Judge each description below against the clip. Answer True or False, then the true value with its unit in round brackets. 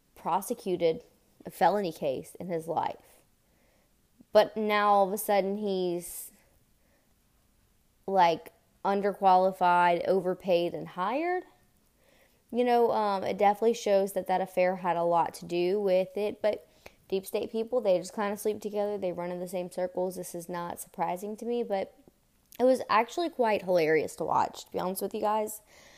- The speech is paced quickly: False (165 wpm)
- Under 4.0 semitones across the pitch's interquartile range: True (3.0 semitones)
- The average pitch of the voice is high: True (195 Hz)